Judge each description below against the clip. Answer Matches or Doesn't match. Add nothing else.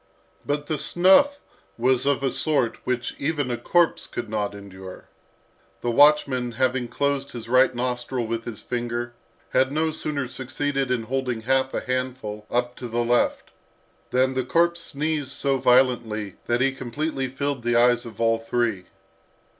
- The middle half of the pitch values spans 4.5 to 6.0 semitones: Doesn't match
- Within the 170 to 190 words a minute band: Doesn't match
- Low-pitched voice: Matches